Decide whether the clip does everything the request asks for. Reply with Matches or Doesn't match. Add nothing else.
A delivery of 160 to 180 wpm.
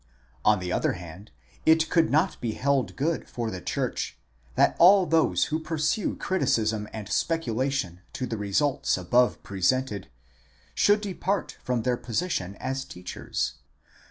Doesn't match